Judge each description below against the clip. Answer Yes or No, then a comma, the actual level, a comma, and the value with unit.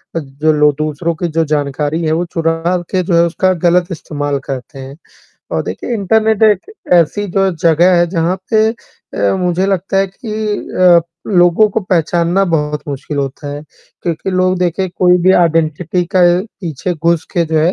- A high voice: No, medium, 170 Hz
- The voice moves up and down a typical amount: Yes, average, 3.2 semitones